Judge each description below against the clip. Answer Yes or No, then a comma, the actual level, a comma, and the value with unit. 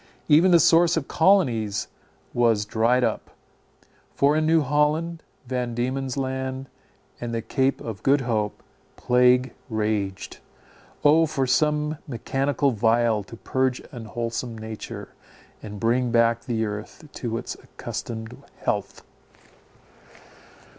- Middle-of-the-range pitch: No, low, 125 Hz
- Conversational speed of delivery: No, slow, 120 wpm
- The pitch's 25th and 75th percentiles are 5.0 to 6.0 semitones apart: No, average, 4.0 semitones